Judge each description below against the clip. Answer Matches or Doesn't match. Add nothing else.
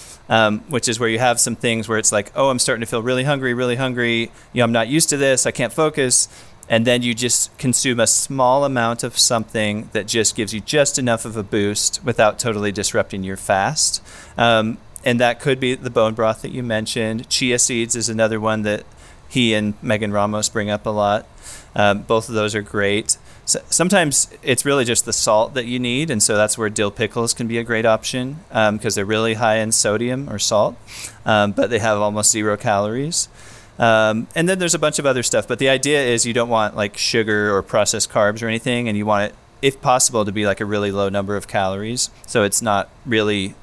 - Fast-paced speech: Matches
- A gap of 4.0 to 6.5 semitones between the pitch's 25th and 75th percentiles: Doesn't match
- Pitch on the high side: Doesn't match